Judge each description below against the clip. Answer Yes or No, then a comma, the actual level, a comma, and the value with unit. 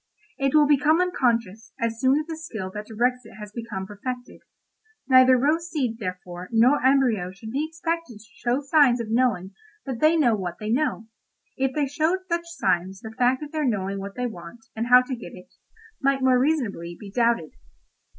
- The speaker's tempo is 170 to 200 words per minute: Yes, average, 190 wpm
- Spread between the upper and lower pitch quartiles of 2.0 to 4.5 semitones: No, average, 5.1 semitones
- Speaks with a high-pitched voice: Yes, high, 245 Hz